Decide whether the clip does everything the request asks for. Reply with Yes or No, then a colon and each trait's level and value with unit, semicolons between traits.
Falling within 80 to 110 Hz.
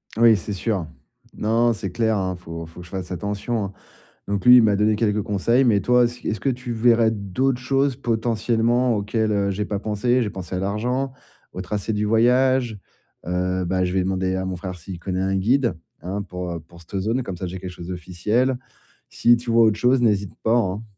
Yes: low, 105 Hz